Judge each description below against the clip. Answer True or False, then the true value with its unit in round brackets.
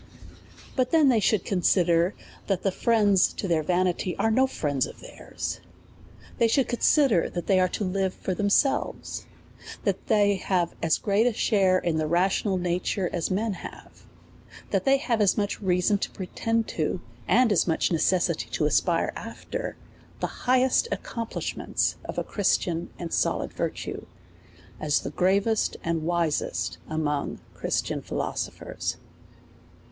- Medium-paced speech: True (150 wpm)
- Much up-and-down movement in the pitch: False (4.1 semitones)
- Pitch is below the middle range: False (190 Hz)